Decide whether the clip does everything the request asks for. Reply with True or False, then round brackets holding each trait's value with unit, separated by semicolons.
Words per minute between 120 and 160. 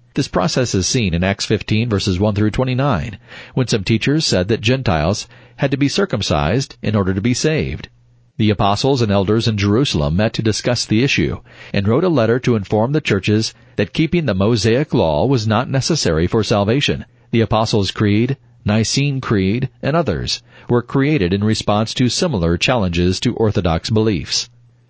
False (175 wpm)